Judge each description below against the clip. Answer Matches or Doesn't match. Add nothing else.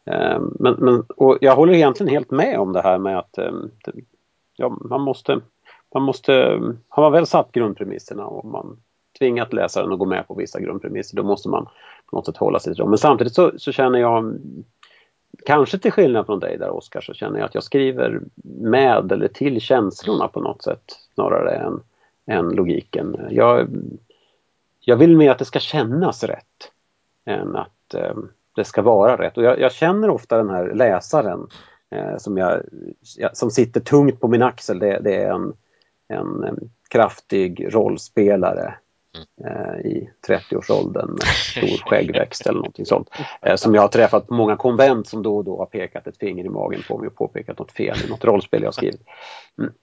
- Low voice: Matches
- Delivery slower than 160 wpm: Doesn't match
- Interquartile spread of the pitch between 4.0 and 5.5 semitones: Matches